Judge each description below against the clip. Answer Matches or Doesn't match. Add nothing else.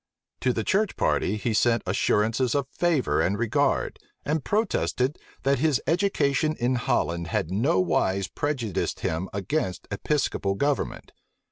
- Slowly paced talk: Matches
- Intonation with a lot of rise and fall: Matches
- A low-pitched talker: Matches